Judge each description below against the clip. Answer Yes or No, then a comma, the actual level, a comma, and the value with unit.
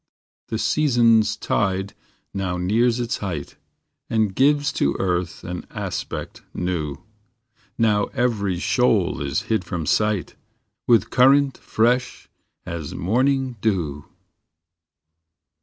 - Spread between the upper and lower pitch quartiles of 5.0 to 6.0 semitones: Yes, average, 5.3 semitones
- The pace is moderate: No, slow, 110 wpm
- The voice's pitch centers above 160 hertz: No, low, 105 Hz